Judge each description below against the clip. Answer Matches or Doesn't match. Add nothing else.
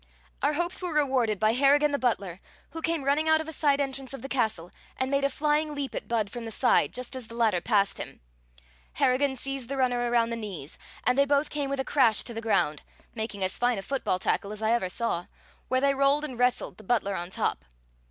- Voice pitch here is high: Matches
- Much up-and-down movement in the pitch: Doesn't match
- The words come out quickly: Matches